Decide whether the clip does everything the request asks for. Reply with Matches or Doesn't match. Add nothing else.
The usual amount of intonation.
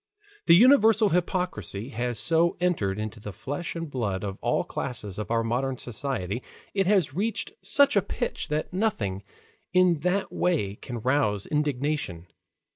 Doesn't match